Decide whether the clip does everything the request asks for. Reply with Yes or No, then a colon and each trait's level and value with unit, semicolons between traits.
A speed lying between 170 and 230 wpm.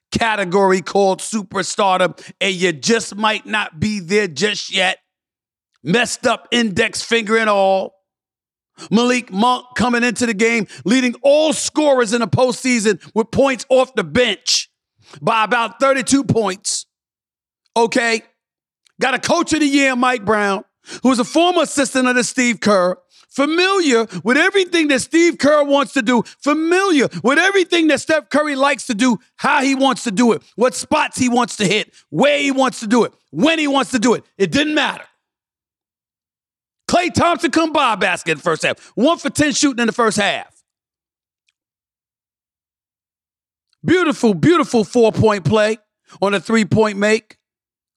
No: average, 160 wpm